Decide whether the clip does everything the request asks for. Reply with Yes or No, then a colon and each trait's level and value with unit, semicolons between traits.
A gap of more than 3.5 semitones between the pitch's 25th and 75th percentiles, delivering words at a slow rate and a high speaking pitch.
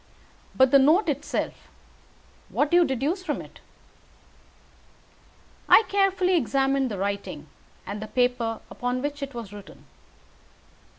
Yes: wide, 5.4 semitones; slow, 125 wpm; very high, 270 Hz